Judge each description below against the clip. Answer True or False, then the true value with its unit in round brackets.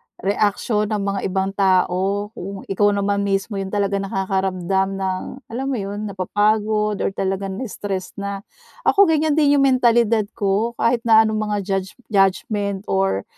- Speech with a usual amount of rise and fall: False (1.8 semitones)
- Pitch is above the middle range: True (200 Hz)